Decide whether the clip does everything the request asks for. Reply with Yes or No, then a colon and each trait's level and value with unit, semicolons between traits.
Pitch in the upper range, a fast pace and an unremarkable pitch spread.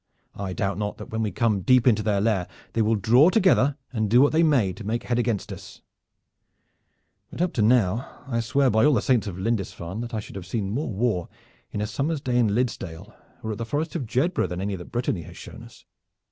No: low, 115 Hz; fast, 230 wpm; average, 4.0 semitones